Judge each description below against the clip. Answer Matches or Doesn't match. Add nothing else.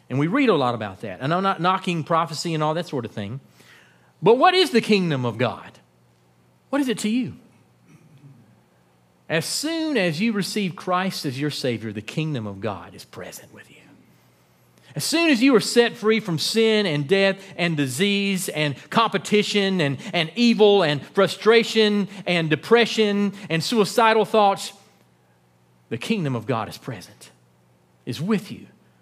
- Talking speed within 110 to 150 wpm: Doesn't match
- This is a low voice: Doesn't match